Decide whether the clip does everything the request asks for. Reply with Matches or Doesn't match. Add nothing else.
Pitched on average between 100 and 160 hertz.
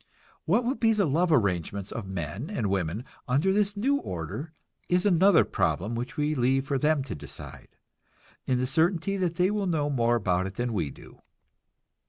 Matches